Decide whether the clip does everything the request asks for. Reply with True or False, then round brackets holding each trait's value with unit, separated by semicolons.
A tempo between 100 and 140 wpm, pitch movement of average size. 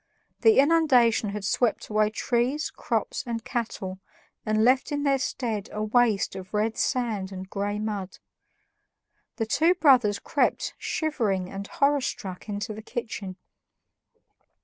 True (135 wpm; 4.1 semitones)